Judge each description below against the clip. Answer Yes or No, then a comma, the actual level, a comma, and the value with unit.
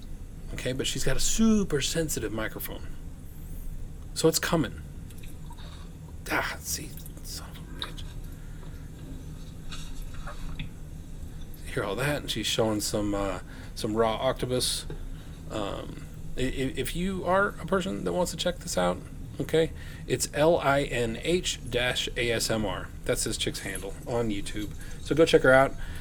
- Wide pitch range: Yes, wide, 8.7 semitones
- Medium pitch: No, low, 110 Hz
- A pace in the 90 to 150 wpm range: Yes, slow, 135 wpm